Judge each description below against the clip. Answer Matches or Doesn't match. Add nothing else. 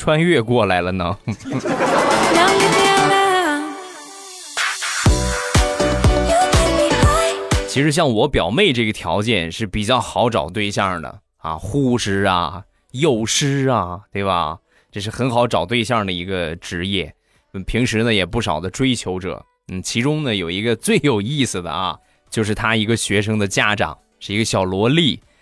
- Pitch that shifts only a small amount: Doesn't match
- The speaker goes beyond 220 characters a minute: Doesn't match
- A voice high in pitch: Doesn't match